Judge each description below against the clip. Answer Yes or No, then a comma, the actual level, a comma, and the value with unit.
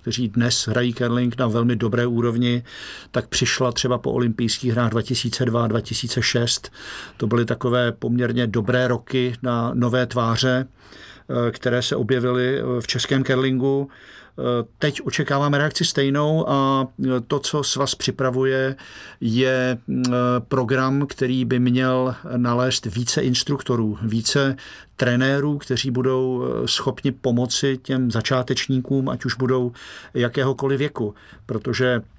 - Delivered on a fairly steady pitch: Yes, narrow, 1.6 semitones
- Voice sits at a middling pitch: No, low, 125 Hz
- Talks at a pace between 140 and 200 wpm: No, slow, 115 wpm